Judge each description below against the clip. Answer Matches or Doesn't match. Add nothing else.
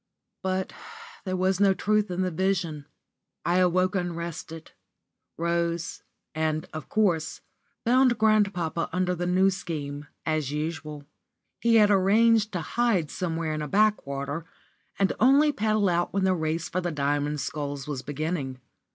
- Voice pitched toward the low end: Doesn't match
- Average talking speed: Matches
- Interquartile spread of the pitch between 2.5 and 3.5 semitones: Doesn't match